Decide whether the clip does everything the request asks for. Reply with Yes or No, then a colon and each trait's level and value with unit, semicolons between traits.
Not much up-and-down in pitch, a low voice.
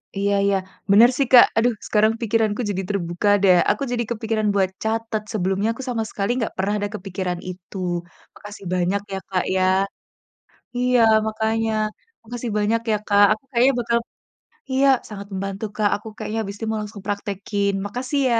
No: narrow, 2.3 semitones; high, 210 Hz